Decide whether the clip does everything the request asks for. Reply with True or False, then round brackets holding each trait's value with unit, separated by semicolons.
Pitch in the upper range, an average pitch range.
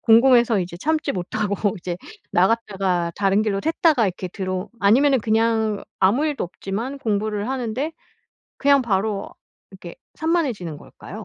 True (215 Hz; 4.8 semitones)